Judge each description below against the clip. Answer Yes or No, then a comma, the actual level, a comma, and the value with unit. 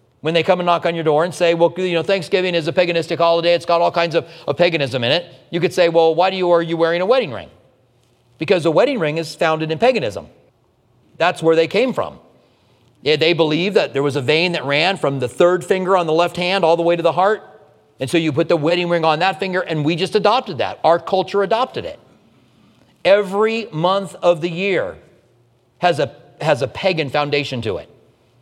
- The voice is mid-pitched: Yes, medium, 170 Hz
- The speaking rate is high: Yes, fast, 230 wpm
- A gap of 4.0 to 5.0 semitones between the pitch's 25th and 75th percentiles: No, narrow, 2.6 semitones